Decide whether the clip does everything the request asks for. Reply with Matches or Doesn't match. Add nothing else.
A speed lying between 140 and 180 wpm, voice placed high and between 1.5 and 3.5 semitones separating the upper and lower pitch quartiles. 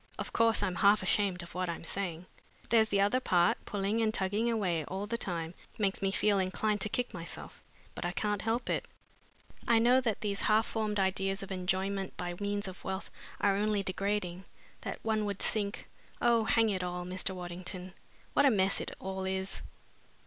Doesn't match